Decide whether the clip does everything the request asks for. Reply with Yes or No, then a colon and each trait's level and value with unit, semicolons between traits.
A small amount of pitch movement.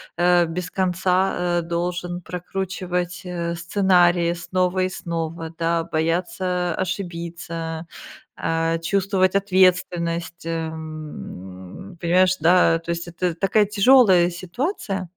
Yes: narrow, 1.8 semitones